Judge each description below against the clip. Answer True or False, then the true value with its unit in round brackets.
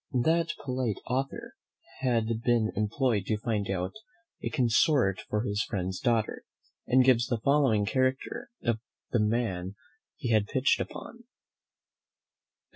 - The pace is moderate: False (125 wpm)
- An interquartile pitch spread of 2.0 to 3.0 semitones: False (3.6 semitones)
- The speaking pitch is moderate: False (115 Hz)